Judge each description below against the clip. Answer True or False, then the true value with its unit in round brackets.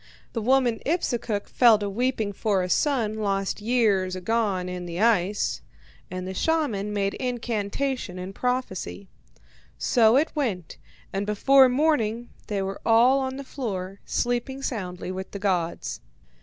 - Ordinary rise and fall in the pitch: True (4.6 semitones)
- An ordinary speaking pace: True (145 wpm)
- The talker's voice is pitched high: True (215 Hz)